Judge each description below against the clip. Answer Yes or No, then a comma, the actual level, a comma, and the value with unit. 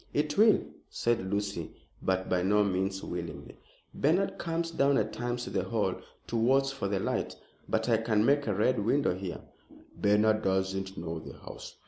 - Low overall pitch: Yes, low, 110 Hz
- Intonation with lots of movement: Yes, wide, 6.0 semitones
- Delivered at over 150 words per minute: Yes, average, 175 wpm